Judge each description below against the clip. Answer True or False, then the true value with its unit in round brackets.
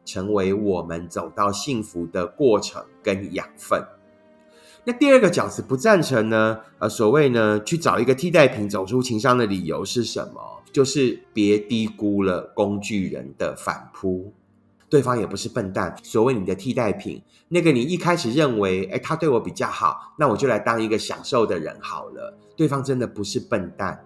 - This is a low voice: True (110 Hz)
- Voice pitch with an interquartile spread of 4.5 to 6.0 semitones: True (5.1 semitones)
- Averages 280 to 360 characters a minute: False (270 characters per minute)